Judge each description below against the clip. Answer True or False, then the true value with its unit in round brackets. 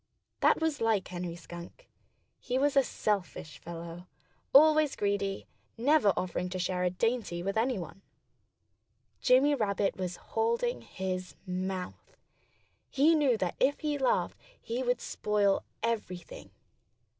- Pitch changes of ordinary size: False (6.7 semitones)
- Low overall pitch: False (205 Hz)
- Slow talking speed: True (125 wpm)